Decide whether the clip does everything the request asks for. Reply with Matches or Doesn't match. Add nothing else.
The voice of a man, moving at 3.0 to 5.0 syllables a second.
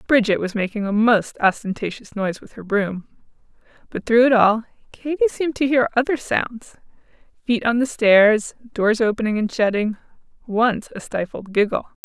Doesn't match